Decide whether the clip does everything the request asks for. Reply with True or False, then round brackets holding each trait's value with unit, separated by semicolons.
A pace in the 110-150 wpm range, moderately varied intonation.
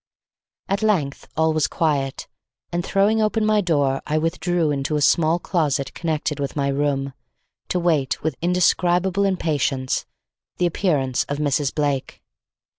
True (140 wpm; 4.0 semitones)